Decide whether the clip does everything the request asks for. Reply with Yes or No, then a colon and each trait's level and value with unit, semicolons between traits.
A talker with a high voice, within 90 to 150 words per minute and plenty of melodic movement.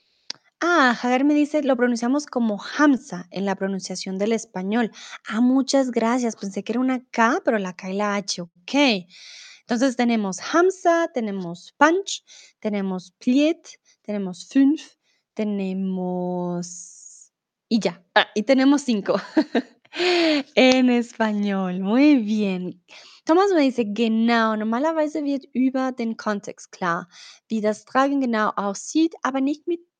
Yes: high, 235 Hz; average, 130 wpm; wide, 5.8 semitones